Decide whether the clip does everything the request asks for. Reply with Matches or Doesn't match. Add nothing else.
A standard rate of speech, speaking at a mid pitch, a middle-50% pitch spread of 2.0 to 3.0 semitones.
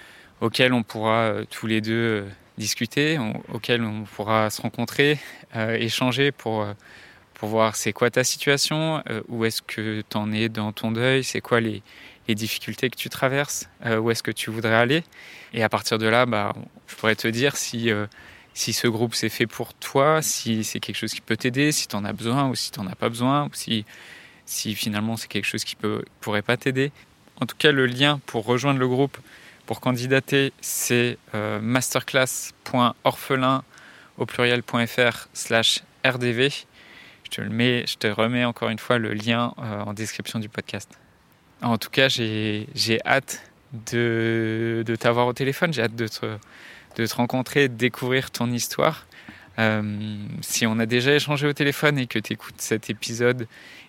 Doesn't match